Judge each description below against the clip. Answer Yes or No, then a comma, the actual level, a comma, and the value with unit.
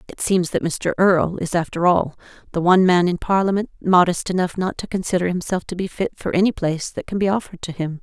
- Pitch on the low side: No, medium, 180 Hz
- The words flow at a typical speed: No, fast, 230 wpm